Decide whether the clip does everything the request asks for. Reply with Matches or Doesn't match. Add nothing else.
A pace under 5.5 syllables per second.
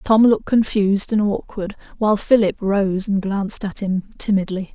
Matches